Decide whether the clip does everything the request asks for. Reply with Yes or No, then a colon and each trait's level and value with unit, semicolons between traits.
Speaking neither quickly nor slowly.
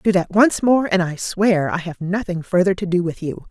No: fast, 255 wpm